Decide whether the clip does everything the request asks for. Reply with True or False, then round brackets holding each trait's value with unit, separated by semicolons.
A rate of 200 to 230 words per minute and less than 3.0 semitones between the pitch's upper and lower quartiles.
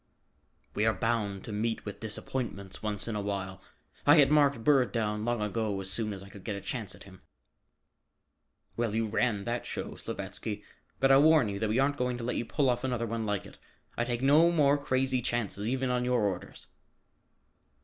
False (205 wpm; 3.7 semitones)